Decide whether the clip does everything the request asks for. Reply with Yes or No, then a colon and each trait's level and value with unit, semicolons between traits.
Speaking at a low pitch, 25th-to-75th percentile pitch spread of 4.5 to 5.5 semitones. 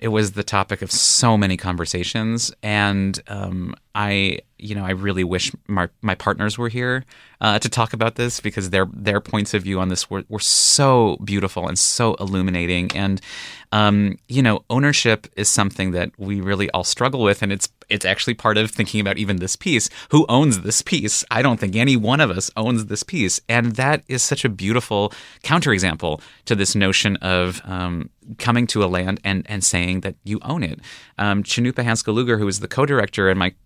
No: low, 105 Hz; average, 3.4 semitones